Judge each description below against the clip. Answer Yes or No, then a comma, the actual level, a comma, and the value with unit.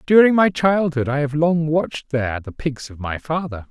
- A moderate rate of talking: No, fast, 210 wpm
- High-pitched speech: No, medium, 150 Hz